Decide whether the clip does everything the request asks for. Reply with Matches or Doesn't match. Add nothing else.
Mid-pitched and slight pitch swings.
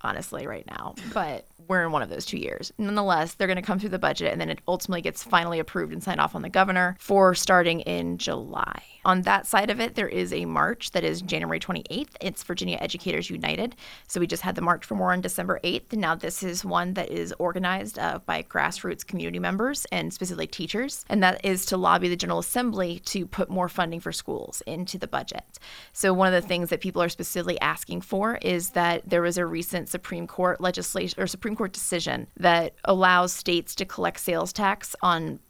Matches